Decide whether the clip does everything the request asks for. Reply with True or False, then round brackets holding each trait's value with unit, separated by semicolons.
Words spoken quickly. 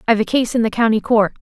True (290 wpm)